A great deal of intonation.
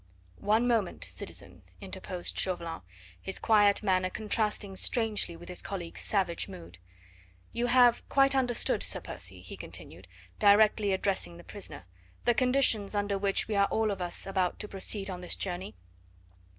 No: average, 3.2 semitones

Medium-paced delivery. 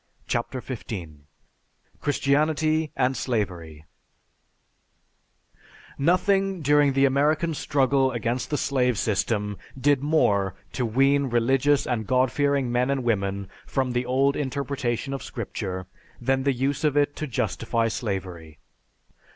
No: slow, 120 wpm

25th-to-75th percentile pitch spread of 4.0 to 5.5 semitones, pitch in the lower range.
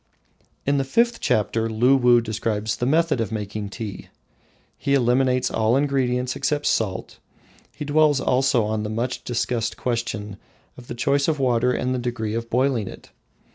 No: average, 3.3 semitones; low, 125 Hz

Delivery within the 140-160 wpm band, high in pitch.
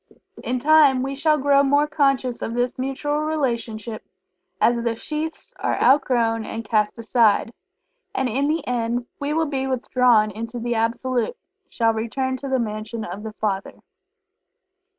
Yes: average, 150 wpm; high, 245 Hz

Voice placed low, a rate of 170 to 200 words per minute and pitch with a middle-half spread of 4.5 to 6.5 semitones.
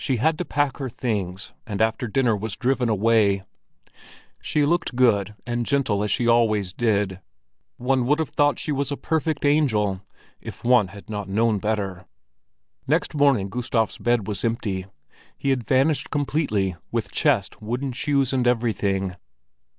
No: low, 115 Hz; average, 155 wpm; average, 4.8 semitones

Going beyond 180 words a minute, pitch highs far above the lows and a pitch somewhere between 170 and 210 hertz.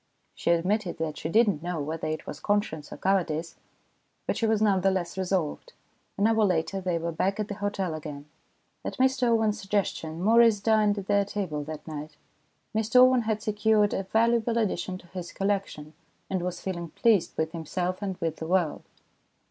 No: average, 190 wpm; average, 4.3 semitones; high, 190 Hz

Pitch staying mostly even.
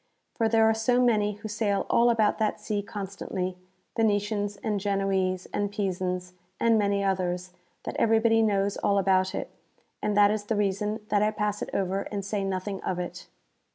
Yes: narrow, 1.9 semitones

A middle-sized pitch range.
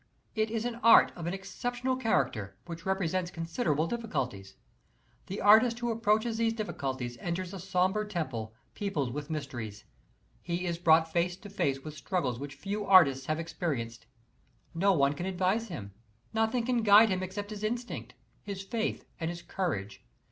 No: wide, 6.5 semitones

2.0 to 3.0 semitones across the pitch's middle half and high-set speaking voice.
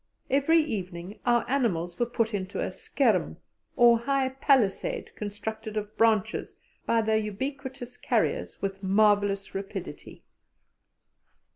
No: average, 3.6 semitones; high, 220 Hz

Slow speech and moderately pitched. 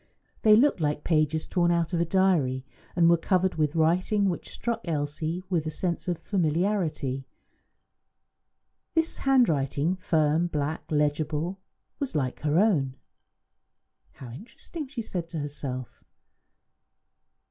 Yes: slow, 125 wpm; medium, 165 Hz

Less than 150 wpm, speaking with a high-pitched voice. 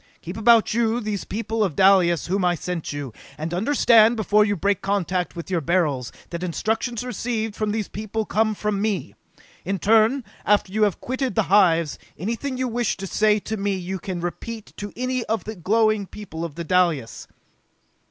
No: average, 185 wpm; high, 205 Hz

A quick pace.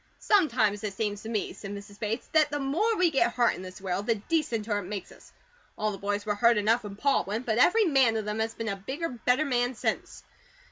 Yes: fast, 240 wpm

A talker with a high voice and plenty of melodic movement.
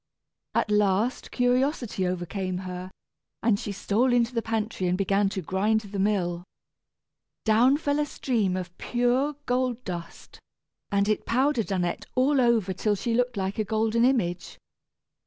No: high, 215 Hz; average, 4.5 semitones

